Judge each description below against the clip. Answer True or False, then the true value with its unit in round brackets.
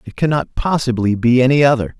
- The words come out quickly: False (180 wpm)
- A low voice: True (130 Hz)